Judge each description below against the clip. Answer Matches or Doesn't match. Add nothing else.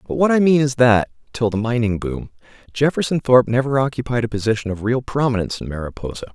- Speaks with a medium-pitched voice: Doesn't match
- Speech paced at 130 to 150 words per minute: Doesn't match